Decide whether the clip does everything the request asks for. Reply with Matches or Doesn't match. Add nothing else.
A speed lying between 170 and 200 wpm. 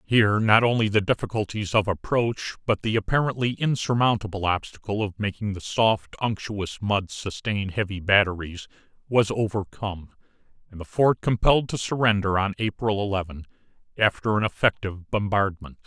Doesn't match